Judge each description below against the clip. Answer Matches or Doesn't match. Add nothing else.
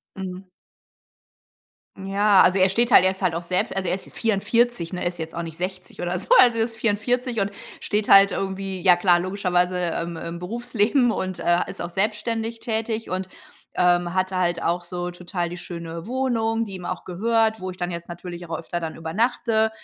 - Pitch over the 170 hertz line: Matches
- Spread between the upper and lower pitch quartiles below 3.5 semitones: Doesn't match